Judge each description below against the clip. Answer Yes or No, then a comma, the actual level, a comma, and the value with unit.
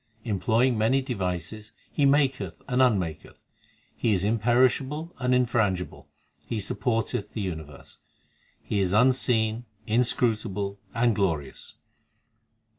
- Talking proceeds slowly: Yes, slow, 105 wpm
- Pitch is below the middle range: Yes, low, 110 Hz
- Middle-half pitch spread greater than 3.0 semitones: Yes, average, 4.1 semitones